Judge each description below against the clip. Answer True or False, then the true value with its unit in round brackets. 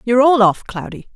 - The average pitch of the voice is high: True (235 Hz)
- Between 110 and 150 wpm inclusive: False (205 wpm)